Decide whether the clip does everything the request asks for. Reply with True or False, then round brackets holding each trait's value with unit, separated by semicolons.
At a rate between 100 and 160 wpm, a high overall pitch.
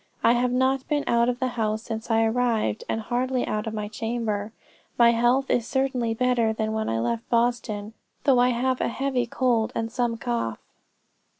False (190 wpm; 235 Hz)